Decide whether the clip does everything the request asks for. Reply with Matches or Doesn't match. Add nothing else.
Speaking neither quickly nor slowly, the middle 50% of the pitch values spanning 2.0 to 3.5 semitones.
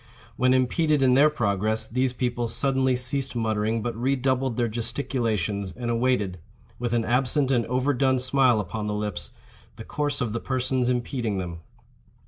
Matches